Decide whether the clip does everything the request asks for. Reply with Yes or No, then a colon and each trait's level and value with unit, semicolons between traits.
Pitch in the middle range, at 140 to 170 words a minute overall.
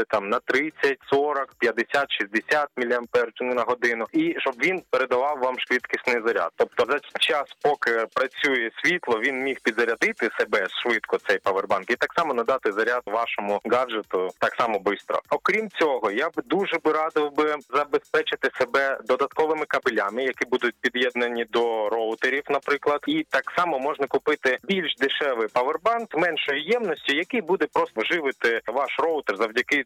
Yes: medium, 150 Hz; average, 150 wpm